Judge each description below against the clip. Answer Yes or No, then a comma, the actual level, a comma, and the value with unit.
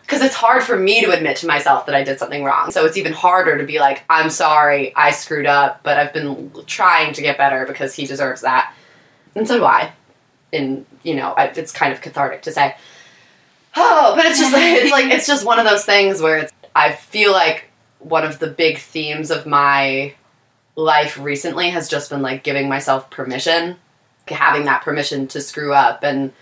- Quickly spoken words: Yes, fast, 210 wpm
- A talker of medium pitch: Yes, medium, 150 Hz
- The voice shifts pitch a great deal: No, average, 3.9 semitones